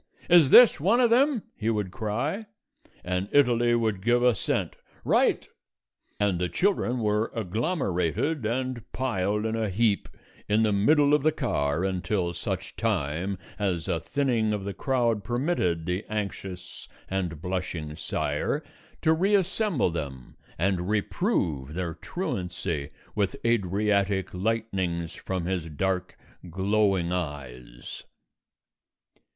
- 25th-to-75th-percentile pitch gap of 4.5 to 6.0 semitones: Yes, average, 5.1 semitones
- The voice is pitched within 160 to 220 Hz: No, low, 100 Hz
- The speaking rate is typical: No, slow, 125 wpm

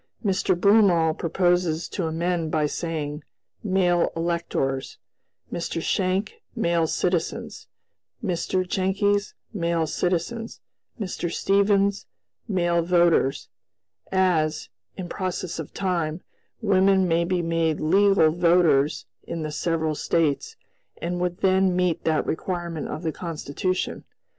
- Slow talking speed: Yes, slow, 110 wpm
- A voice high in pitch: No, medium, 175 Hz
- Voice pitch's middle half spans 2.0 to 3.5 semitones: Yes, narrow, 2.4 semitones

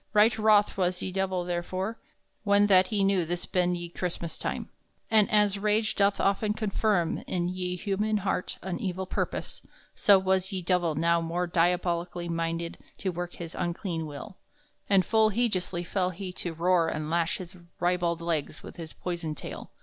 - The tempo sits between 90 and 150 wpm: No, average, 170 wpm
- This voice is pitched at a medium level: Yes, medium, 180 Hz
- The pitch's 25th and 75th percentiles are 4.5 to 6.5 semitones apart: No, narrow, 2.5 semitones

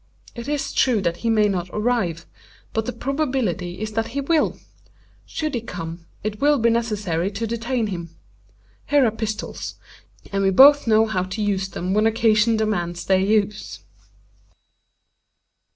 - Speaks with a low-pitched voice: No, high, 215 Hz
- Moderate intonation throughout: Yes, average, 3.6 semitones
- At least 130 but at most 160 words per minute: Yes, average, 155 wpm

